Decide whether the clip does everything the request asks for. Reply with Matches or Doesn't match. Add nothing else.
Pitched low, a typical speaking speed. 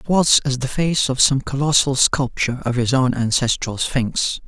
Matches